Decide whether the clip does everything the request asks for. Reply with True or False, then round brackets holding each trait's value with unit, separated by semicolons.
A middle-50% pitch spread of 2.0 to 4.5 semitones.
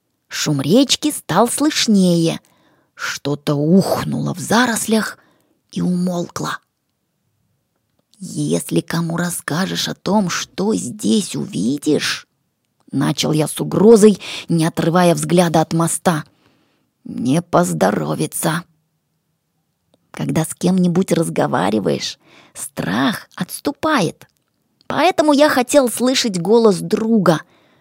False (5.6 semitones)